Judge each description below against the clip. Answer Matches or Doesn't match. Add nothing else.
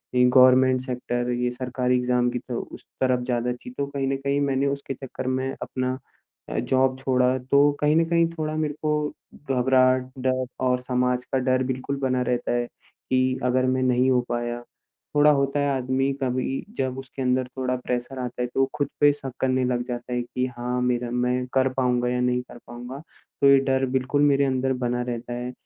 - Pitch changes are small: Matches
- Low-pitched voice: Matches